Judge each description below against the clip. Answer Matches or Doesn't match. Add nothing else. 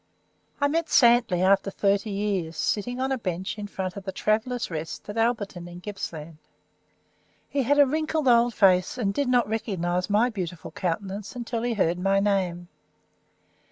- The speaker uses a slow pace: Doesn't match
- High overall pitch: Matches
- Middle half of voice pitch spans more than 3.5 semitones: Matches